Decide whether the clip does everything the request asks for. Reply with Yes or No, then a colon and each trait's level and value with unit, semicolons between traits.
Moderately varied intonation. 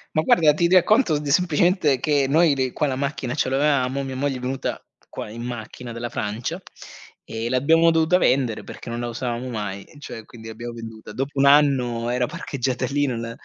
Yes: average, 3.8 semitones